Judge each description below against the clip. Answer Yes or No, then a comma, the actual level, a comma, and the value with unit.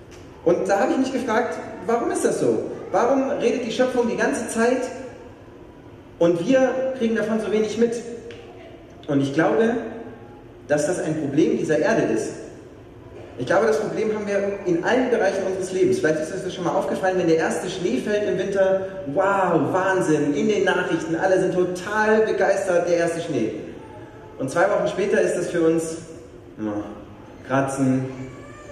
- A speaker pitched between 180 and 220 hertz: Yes, high, 190 Hz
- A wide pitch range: Yes, wide, 6.1 semitones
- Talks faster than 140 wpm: Yes, average, 170 wpm